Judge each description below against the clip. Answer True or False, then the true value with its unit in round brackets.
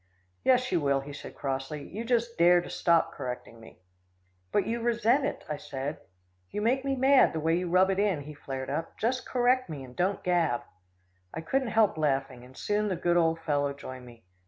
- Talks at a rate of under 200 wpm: False (205 wpm)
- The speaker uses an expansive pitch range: True (8.2 semitones)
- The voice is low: False (170 Hz)